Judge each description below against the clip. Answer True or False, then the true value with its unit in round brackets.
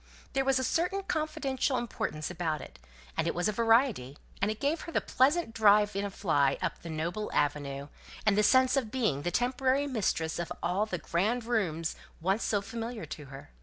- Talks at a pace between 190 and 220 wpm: True (200 wpm)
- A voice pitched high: True (210 Hz)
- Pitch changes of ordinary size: False (7.4 semitones)